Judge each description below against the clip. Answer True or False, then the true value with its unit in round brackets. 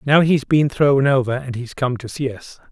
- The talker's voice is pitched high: False (135 Hz)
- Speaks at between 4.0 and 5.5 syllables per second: True (4.8 syllables/s)